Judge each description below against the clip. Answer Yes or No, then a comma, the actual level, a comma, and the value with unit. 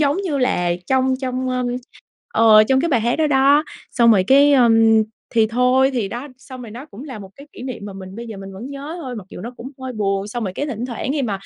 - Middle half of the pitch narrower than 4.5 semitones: Yes, average, 3.9 semitones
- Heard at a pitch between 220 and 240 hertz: No, very high, 250 Hz